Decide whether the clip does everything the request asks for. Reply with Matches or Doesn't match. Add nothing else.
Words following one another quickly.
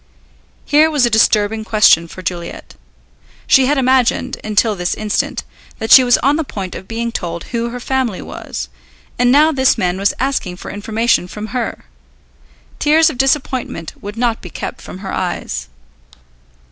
Doesn't match